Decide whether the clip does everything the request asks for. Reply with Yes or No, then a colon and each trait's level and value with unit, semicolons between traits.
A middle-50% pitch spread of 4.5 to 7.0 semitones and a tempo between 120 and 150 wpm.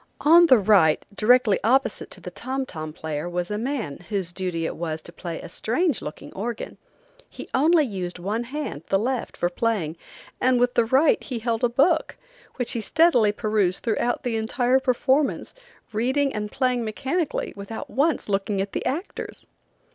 No: average, 5.3 semitones; average, 175 wpm